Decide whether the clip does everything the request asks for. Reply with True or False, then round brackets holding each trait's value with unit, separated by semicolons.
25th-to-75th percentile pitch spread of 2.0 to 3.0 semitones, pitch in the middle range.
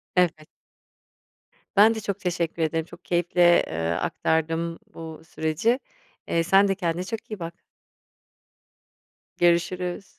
True (2.4 semitones; 175 Hz)